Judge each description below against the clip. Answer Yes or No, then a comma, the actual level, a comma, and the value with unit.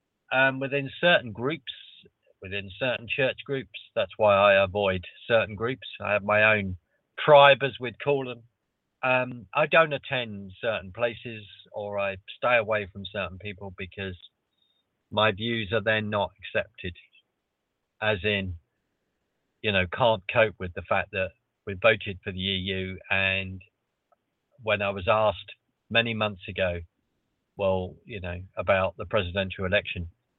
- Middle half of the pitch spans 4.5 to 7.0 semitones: No, average, 3.5 semitones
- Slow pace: No, average, 145 wpm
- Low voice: Yes, low, 105 Hz